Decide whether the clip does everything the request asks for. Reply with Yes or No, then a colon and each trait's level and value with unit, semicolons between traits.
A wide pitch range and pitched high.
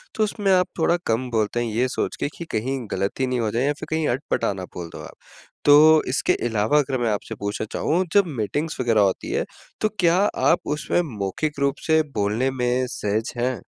No: wide, 5.8 semitones; low, 130 Hz